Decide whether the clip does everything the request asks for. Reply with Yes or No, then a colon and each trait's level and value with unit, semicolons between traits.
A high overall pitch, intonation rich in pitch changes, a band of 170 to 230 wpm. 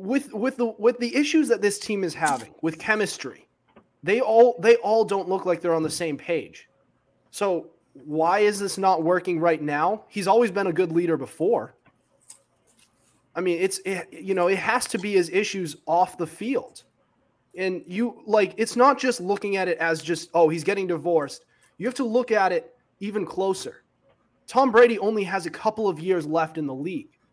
No: high, 195 Hz; average, 4.6 semitones; average, 200 wpm